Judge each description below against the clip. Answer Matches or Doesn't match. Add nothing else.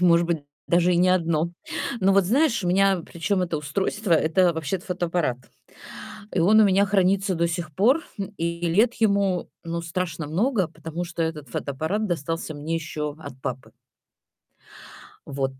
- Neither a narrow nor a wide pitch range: Matches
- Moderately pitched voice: Matches